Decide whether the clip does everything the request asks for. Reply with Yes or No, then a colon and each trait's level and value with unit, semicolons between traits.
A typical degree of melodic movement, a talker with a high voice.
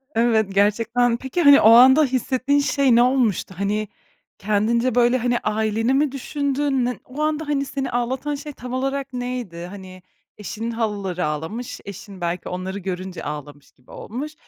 Yes: average, 4.8 semitones; high, 235 Hz